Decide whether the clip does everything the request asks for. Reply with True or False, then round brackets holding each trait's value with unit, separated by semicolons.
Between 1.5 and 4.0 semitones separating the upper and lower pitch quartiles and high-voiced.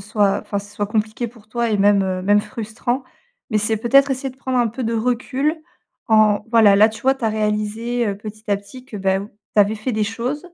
True (2.7 semitones; 220 Hz)